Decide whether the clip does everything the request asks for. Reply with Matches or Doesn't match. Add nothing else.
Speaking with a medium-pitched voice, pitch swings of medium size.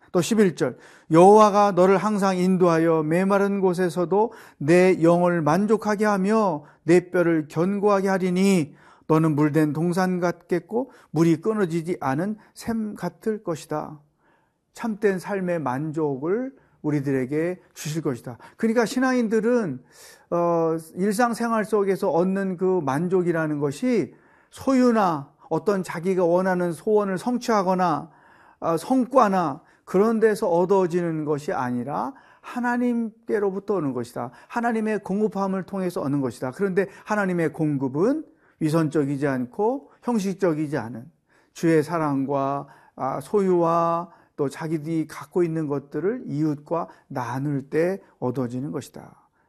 Matches